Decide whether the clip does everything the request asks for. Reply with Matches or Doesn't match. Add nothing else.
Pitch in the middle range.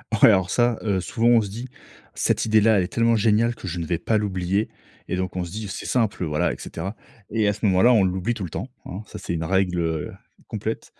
Doesn't match